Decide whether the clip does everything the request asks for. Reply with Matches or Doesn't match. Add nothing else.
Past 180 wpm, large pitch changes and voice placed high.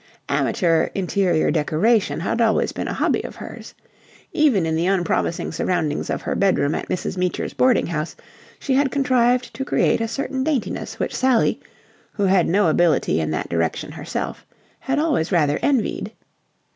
Doesn't match